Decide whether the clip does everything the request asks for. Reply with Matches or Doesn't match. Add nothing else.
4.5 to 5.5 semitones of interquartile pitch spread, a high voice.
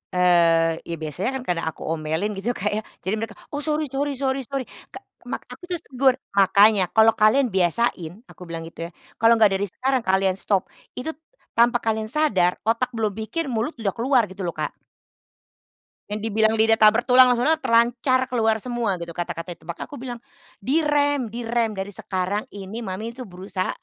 Matches